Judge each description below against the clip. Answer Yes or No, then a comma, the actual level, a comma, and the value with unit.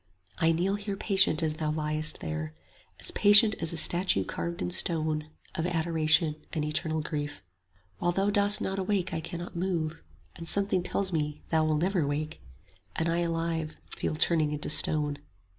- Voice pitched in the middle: Yes, medium, 165 Hz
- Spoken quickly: No, average, 175 wpm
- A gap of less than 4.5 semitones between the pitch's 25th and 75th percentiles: Yes, average, 2.8 semitones